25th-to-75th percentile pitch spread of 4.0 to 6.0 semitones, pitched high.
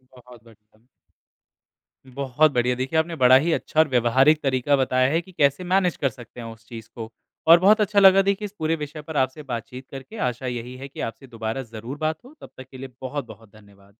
No: average, 4.6 semitones; low, 130 Hz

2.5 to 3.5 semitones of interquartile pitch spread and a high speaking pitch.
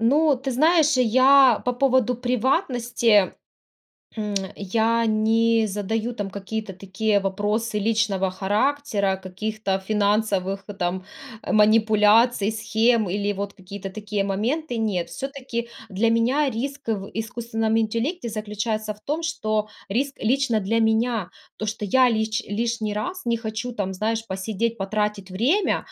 Yes: average, 2.9 semitones; high, 220 Hz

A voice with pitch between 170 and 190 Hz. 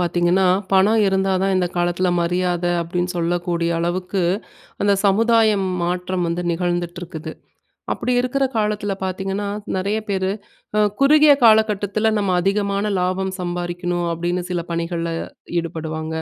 Yes: medium, 185 Hz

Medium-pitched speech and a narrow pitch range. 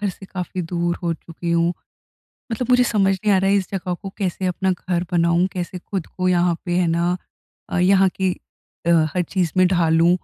Yes: medium, 180 Hz; narrow, 1.8 semitones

